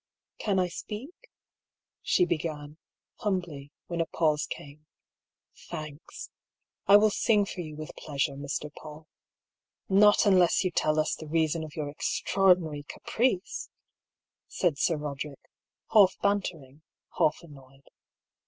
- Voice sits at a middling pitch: Yes, medium, 160 Hz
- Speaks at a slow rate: Yes, slow, 130 wpm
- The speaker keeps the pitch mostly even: No, average, 4.2 semitones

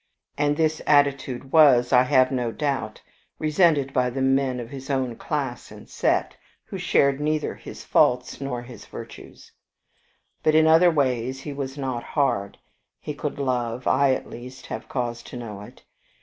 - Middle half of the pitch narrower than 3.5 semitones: Yes, average, 2.7 semitones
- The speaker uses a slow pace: No, average, 165 wpm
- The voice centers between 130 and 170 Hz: Yes, low, 135 Hz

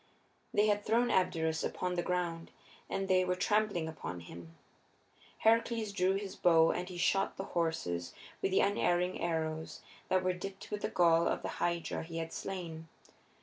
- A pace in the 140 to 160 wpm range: No, average, 170 wpm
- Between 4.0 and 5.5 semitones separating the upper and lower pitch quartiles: No, average, 2.9 semitones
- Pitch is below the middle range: No, medium, 180 Hz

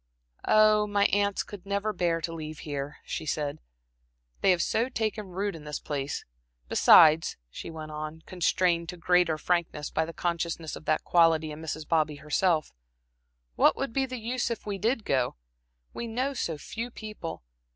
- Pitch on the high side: No, medium, 170 Hz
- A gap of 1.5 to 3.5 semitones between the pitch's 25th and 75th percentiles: No, average, 5.2 semitones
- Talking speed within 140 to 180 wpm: Yes, average, 170 wpm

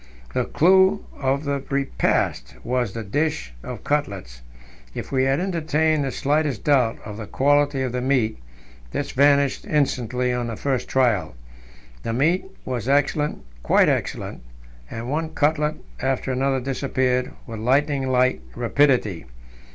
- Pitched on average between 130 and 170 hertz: Yes, low, 135 Hz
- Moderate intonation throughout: Yes, average, 3.1 semitones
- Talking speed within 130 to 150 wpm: Yes, average, 140 wpm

